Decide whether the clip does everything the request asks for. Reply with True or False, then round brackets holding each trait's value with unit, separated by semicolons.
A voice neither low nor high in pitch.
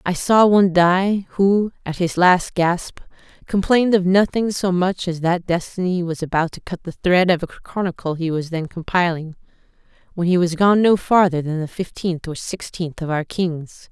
True (180 Hz)